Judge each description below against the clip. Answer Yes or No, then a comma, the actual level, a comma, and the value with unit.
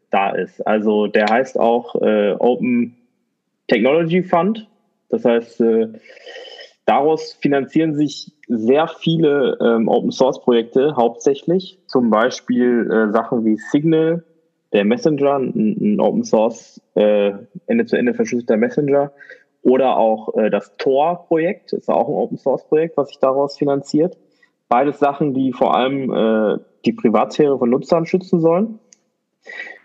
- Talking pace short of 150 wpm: Yes, average, 140 wpm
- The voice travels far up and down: Yes, wide, 8.0 semitones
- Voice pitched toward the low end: No, medium, 150 Hz